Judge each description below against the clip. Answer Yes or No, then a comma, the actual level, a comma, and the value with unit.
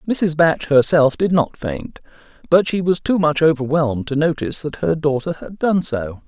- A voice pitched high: No, medium, 155 Hz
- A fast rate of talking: No, average, 190 wpm